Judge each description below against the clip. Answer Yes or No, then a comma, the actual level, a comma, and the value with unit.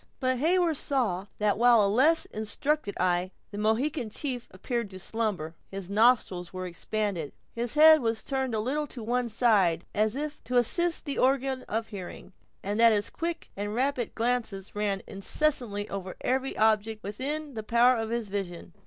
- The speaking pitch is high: Yes, high, 225 Hz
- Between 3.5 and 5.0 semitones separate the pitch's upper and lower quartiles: Yes, average, 4.4 semitones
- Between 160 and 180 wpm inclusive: Yes, average, 175 wpm